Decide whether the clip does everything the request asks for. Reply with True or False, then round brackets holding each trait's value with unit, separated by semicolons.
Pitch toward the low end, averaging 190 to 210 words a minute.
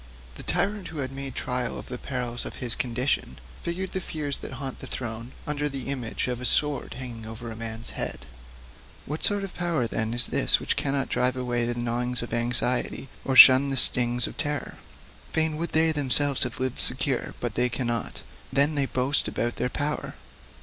True (130 Hz; 195 wpm)